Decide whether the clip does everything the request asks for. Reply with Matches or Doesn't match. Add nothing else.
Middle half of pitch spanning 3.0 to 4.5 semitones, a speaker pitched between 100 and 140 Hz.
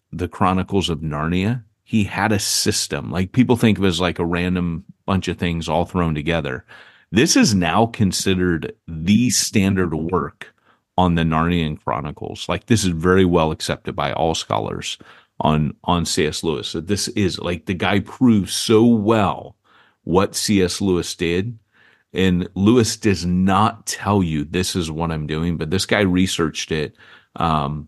Doesn't match